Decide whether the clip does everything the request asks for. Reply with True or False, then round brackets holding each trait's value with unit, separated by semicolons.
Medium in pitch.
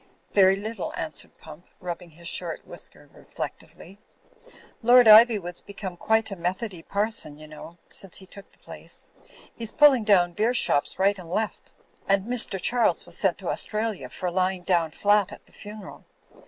False (195 Hz)